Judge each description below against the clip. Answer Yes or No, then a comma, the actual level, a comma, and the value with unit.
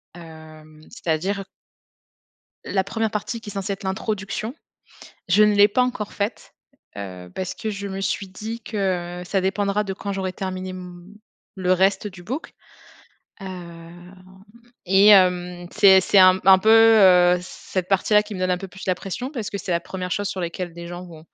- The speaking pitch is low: No, high, 190 Hz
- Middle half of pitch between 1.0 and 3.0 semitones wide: Yes, narrow, 2.4 semitones